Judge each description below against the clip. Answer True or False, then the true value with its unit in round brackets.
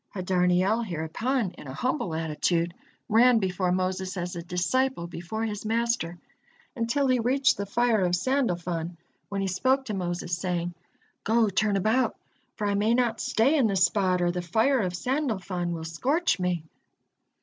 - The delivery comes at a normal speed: True (160 wpm)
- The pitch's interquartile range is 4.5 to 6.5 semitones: True (4.9 semitones)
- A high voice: True (195 Hz)